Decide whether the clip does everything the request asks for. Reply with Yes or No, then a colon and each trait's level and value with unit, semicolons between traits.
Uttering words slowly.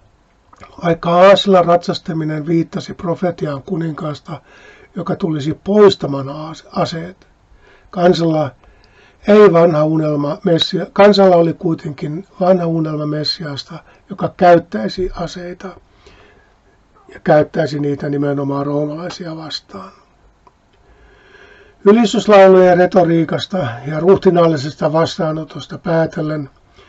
Yes: slow, 80 wpm